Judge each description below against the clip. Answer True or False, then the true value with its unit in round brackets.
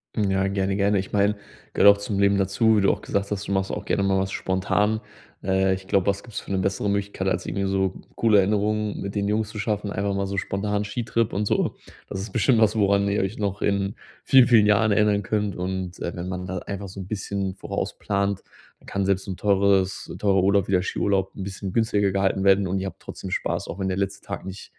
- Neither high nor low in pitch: False (100 Hz)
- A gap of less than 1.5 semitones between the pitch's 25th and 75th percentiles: True (1.1 semitones)